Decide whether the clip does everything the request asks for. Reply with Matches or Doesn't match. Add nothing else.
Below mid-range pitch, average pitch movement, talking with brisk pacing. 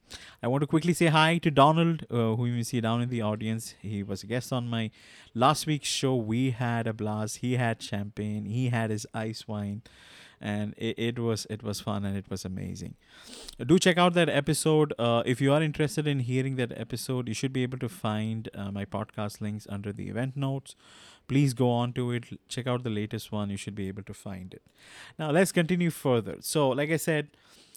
Matches